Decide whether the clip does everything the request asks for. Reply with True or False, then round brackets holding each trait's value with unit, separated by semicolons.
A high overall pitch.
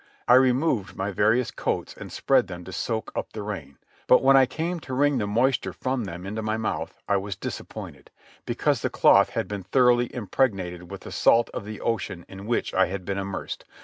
False (105 Hz)